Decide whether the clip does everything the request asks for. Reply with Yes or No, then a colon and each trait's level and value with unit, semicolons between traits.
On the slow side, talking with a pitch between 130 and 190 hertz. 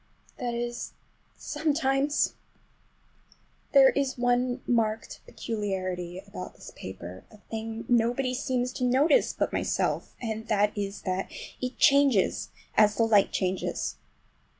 No: slow, 120 wpm; high, 230 Hz